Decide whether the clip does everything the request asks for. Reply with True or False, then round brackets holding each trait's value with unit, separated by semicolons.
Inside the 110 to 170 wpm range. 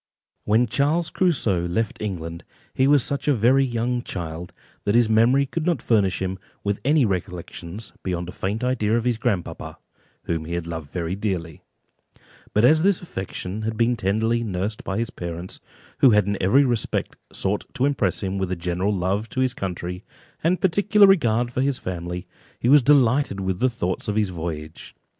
False (180 wpm)